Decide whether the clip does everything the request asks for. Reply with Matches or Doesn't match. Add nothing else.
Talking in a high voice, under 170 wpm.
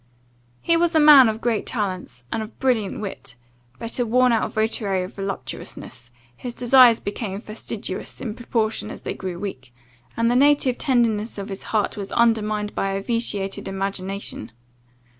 Matches